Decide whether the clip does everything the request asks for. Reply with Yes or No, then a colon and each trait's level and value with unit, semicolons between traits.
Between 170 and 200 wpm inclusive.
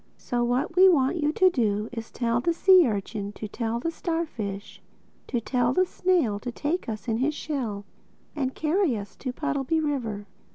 Yes: average, 190 wpm